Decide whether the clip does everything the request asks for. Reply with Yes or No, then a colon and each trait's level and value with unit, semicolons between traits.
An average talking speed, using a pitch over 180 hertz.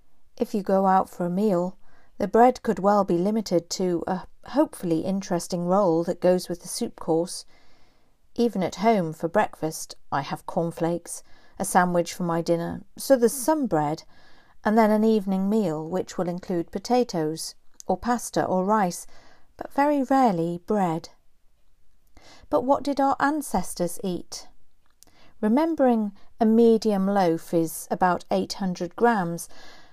Yes: average, 145 wpm; high, 190 Hz